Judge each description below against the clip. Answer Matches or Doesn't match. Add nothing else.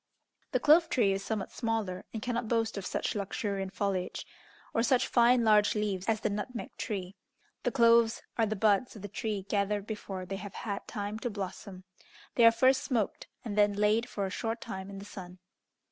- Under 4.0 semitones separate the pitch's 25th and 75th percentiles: Matches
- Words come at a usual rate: Matches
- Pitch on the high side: Matches